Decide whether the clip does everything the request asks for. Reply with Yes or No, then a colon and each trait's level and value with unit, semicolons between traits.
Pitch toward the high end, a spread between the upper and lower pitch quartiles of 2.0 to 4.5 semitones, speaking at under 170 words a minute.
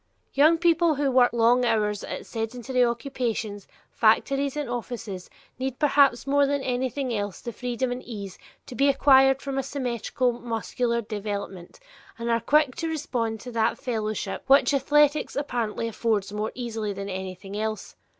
Yes: high, 245 Hz; average, 3.8 semitones; average, 155 wpm